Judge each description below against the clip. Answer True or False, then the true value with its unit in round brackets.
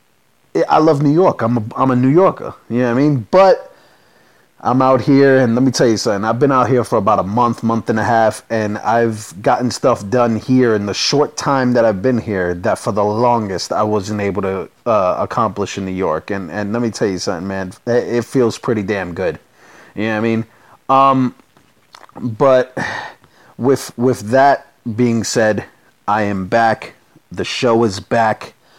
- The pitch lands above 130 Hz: False (115 Hz)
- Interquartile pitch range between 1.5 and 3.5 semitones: True (3.1 semitones)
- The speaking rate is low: False (200 wpm)